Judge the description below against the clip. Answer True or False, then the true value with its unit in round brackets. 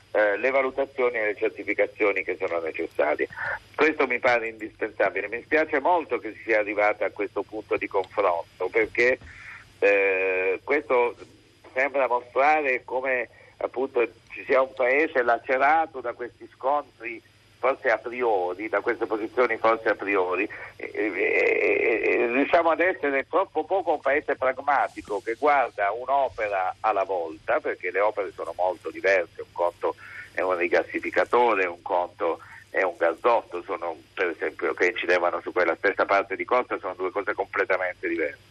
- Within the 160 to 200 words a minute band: False (150 wpm)